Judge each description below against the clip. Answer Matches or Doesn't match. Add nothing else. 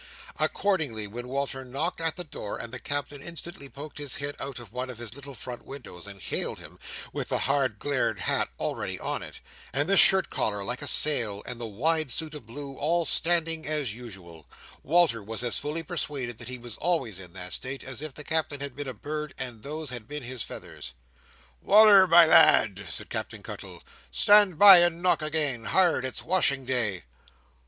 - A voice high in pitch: Doesn't match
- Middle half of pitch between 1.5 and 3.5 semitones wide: Doesn't match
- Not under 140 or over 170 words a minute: Doesn't match